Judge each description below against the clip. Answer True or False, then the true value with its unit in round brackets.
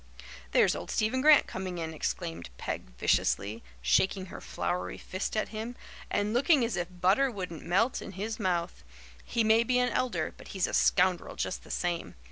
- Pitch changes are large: False (4.6 semitones)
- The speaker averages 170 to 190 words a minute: True (180 wpm)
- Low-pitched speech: False (190 Hz)